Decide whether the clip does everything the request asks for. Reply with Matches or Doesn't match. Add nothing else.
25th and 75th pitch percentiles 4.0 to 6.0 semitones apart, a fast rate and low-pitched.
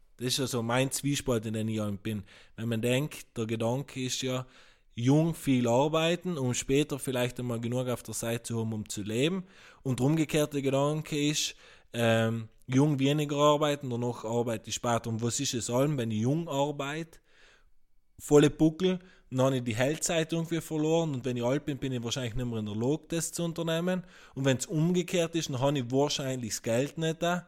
Matches